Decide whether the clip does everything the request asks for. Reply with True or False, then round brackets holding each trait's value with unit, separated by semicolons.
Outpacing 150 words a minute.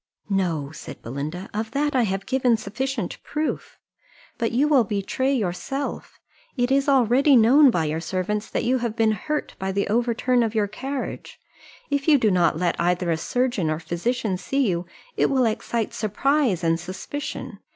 True (170 wpm)